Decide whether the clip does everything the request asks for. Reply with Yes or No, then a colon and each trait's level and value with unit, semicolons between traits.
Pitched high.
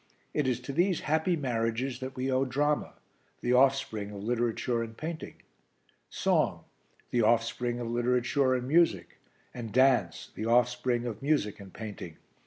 No: low, 125 Hz